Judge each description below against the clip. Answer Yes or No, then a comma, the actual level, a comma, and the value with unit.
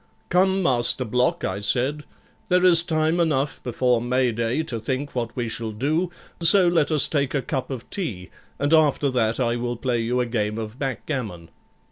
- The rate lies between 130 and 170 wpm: No, average, 185 wpm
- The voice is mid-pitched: No, low, 130 Hz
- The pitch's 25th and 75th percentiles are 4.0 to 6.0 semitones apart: Yes, average, 4.9 semitones